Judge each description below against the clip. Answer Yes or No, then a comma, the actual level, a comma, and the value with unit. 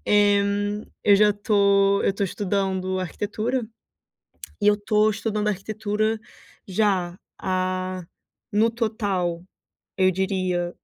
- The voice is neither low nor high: No, high, 200 Hz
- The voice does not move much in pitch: Yes, narrow, 2.0 semitones